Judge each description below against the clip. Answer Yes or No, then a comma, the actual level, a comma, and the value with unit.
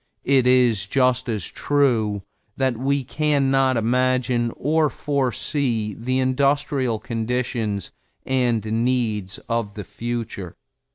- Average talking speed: No, slow, 110 wpm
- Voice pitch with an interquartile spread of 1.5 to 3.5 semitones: Yes, average, 2.9 semitones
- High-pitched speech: No, low, 125 Hz